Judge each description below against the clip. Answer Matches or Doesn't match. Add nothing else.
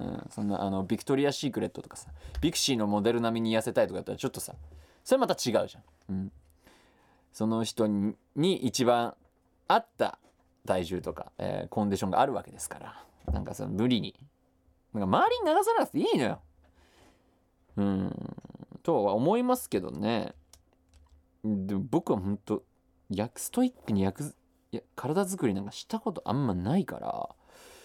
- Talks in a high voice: Doesn't match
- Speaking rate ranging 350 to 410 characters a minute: Doesn't match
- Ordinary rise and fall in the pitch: Doesn't match